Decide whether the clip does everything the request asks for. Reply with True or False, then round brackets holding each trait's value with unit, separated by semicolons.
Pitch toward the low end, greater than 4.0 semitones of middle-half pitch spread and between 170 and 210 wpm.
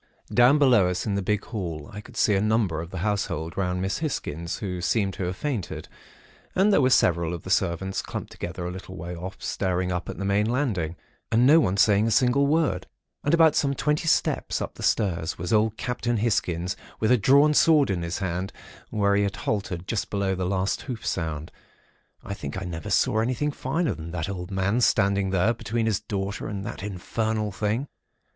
True (100 Hz; 4.5 semitones; 205 wpm)